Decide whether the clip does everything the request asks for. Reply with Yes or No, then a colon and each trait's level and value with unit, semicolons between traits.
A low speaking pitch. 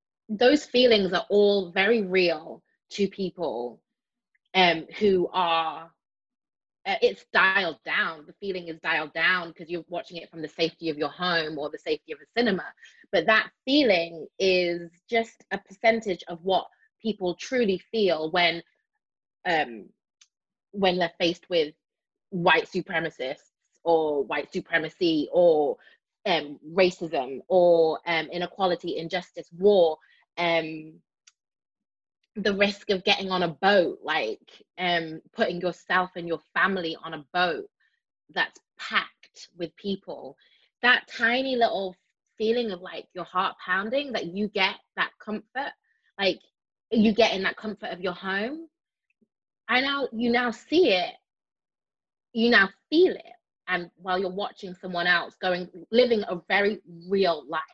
No: medium, 185 Hz